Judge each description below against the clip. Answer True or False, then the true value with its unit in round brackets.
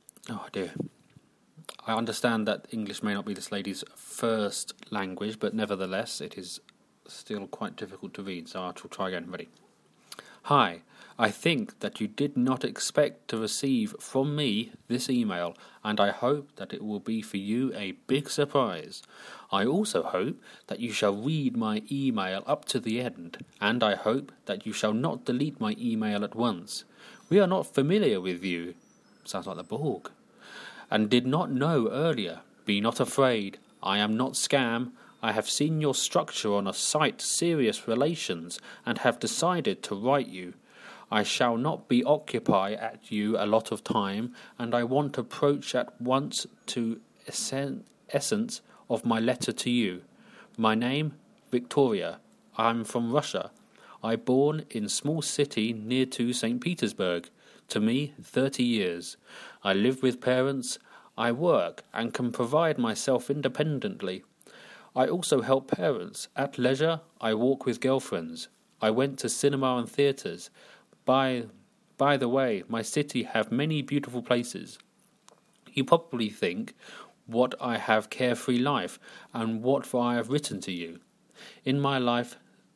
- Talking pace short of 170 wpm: True (155 wpm)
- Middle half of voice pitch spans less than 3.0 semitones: False (4.3 semitones)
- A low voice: True (125 Hz)